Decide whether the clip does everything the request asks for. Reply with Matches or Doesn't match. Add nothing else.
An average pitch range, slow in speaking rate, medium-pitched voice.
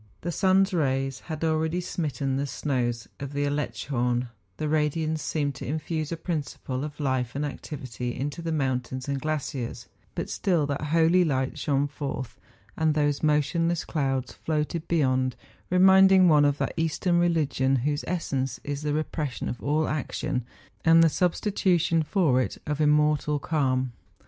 Doesn't match